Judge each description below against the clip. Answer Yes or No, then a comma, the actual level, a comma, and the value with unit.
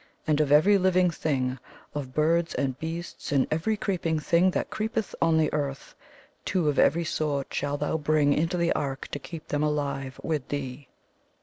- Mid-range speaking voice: Yes, medium, 155 Hz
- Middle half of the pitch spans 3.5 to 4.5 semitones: No, average, 2.9 semitones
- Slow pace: No, average, 185 wpm